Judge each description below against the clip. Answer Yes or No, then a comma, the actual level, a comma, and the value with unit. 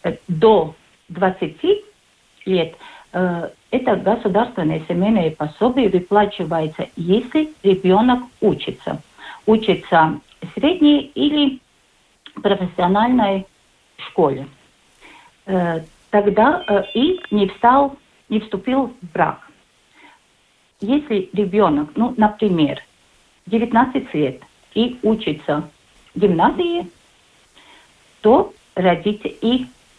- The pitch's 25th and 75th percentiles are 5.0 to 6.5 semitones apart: Yes, average, 5.3 semitones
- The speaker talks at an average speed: No, slow, 75 wpm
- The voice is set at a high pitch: Yes, high, 210 Hz